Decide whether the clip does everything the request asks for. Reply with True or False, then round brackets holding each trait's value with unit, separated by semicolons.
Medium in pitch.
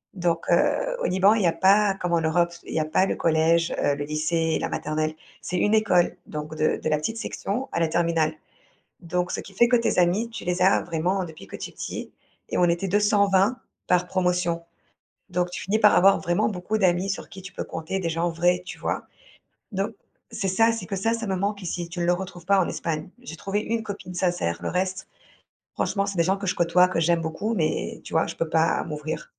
True (180 Hz)